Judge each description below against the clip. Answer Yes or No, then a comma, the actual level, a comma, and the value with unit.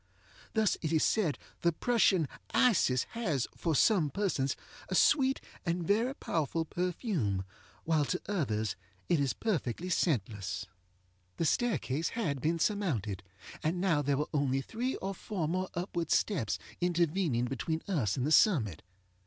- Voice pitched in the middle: Yes, medium, 165 Hz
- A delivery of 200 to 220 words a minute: No, average, 145 wpm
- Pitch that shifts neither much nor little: No, wide, 6.2 semitones